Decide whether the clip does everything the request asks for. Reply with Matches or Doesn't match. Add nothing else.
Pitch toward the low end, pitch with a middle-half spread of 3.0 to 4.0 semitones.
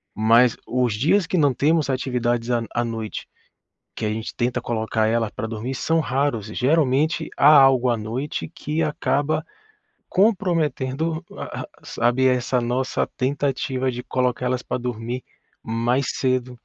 Matches